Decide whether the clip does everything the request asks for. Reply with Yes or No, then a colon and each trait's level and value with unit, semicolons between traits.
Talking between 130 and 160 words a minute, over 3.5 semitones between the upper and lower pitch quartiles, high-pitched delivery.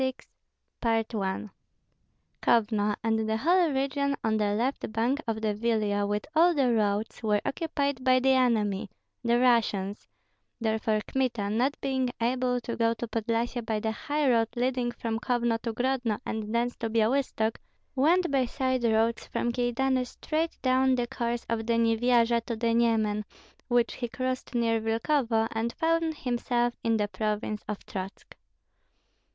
No: average, 155 wpm; average, 2.7 semitones; high, 235 Hz